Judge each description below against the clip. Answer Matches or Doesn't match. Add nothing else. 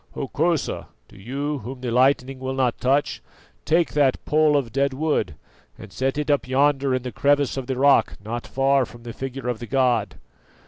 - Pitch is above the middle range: Doesn't match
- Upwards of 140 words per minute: Matches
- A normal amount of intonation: Doesn't match